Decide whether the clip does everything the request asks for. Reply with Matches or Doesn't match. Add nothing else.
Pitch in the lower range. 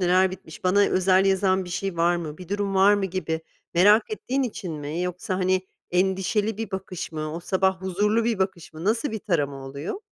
Doesn't match